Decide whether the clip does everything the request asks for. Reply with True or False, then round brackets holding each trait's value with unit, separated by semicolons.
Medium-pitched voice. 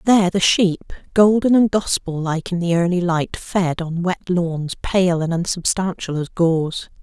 True (175 Hz)